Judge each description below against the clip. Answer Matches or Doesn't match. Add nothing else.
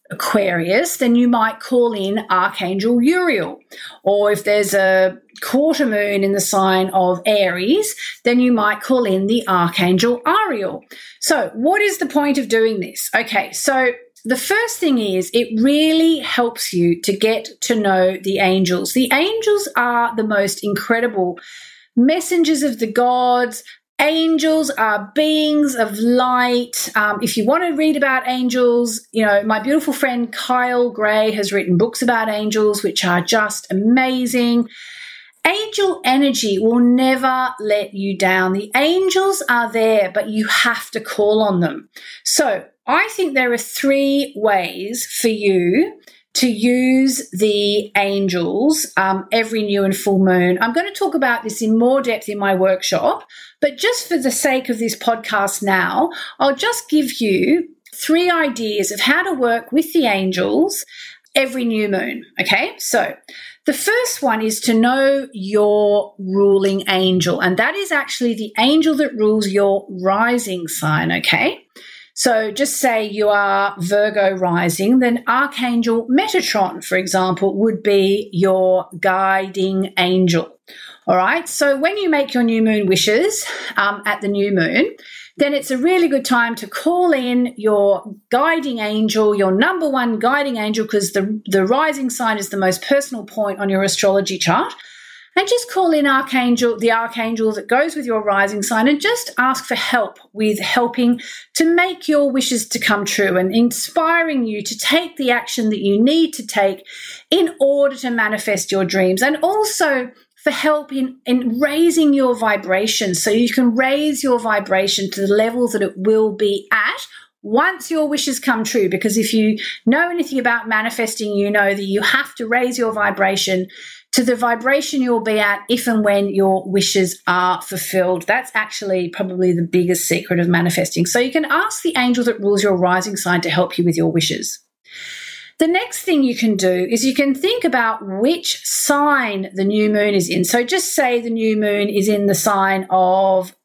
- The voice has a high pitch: Matches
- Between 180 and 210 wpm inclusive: Doesn't match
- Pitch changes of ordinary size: Doesn't match